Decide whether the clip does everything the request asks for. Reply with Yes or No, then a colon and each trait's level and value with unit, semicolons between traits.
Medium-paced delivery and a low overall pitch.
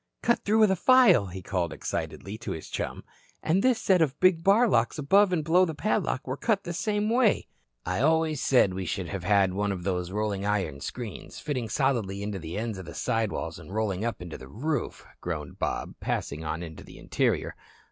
No: fast, 210 wpm; low, 115 Hz